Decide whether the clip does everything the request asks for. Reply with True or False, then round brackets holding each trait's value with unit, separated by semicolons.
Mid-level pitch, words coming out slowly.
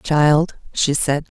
True (150 Hz; 130 wpm)